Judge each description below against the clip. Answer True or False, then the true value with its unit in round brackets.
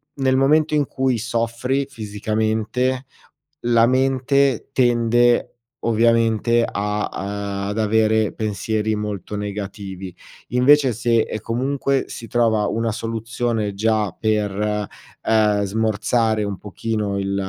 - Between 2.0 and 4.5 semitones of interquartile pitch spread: True (2.6 semitones)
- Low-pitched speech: True (110 Hz)